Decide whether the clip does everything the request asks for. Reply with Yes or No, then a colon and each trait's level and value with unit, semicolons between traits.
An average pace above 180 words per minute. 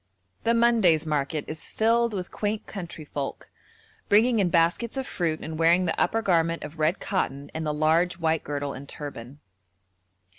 No: average, 160 wpm